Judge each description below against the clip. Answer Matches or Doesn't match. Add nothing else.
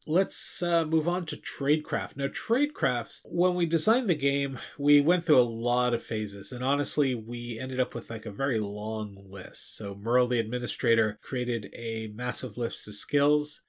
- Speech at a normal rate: Matches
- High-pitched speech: Doesn't match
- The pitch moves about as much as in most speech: Matches